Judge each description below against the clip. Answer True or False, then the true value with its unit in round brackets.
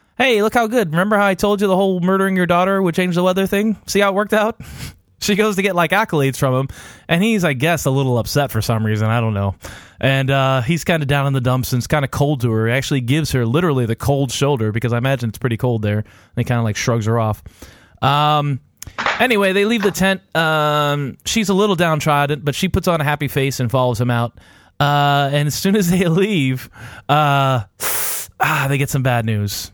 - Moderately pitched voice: True (145 Hz)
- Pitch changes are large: True (6.8 semitones)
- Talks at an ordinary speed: False (240 wpm)